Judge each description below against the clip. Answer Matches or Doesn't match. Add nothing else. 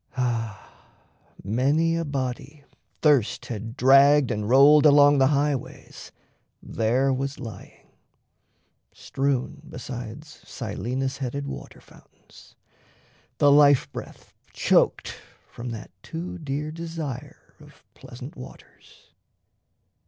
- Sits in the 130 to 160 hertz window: Matches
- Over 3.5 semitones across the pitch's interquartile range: Doesn't match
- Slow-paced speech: Matches